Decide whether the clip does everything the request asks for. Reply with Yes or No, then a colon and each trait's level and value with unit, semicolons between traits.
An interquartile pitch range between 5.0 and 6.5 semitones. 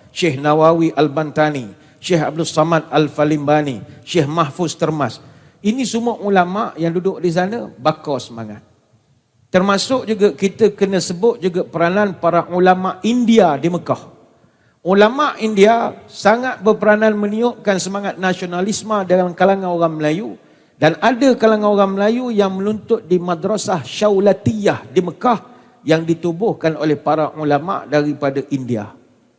Yes: average, 5.3 semitones